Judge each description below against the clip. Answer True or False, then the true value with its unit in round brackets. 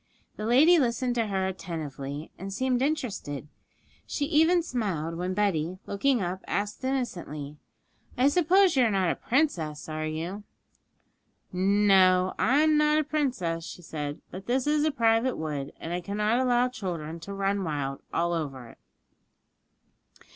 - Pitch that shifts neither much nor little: False (7.6 semitones)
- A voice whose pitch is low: False (200 Hz)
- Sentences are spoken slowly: False (150 wpm)